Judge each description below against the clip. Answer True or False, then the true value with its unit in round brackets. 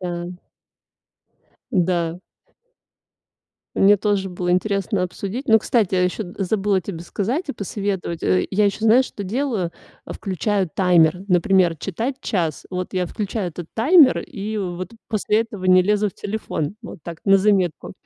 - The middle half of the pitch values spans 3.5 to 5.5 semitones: False (2.9 semitones)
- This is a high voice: True (195 Hz)